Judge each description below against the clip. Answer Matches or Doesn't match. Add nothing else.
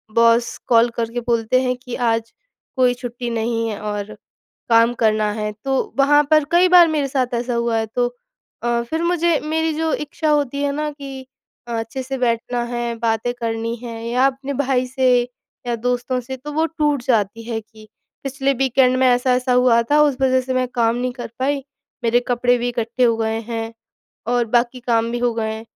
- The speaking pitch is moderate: Doesn't match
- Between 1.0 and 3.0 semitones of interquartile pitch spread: Matches